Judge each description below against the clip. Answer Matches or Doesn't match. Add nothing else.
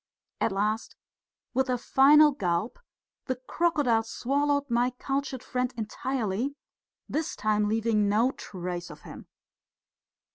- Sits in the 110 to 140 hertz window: Doesn't match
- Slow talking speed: Matches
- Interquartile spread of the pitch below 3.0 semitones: Doesn't match